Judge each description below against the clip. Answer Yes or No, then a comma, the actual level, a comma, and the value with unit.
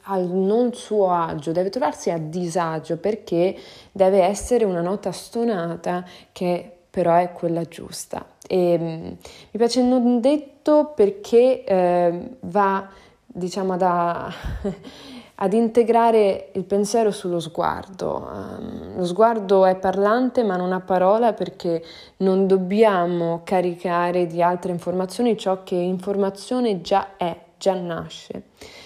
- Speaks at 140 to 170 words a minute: No, average, 120 wpm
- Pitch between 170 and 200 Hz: Yes, high, 190 Hz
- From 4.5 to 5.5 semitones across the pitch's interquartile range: No, average, 3.6 semitones